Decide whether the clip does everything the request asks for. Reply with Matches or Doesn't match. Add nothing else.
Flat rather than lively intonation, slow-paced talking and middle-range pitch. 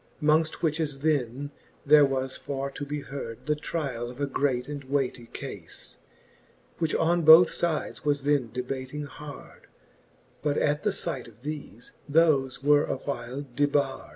Doesn't match